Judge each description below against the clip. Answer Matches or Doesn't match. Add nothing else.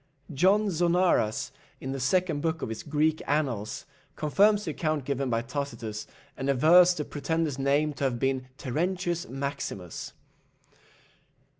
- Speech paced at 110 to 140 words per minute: Matches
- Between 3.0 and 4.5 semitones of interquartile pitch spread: Matches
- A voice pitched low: Doesn't match